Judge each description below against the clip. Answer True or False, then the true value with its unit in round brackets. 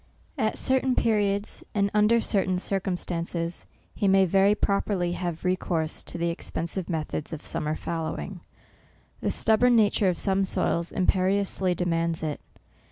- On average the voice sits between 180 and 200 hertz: True (185 Hz)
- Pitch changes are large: False (3.0 semitones)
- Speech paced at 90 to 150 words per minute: True (145 wpm)